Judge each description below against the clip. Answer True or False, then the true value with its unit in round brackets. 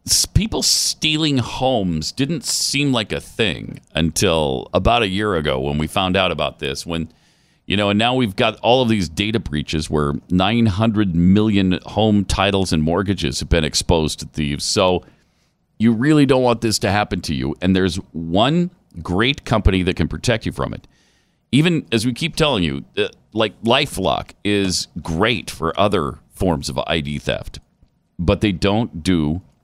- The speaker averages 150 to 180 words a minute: True (170 wpm)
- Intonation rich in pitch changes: True (5.9 semitones)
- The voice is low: True (95 Hz)